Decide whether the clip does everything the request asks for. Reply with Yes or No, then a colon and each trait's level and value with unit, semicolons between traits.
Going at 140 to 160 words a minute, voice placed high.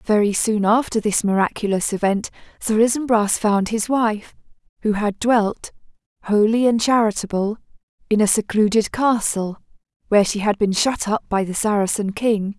Yes: average, 150 wpm; high, 215 Hz